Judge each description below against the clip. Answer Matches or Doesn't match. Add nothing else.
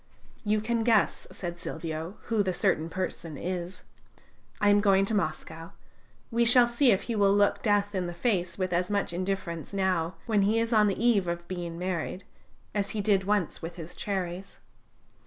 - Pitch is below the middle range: Doesn't match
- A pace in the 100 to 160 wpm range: Doesn't match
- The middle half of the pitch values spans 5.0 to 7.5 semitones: Doesn't match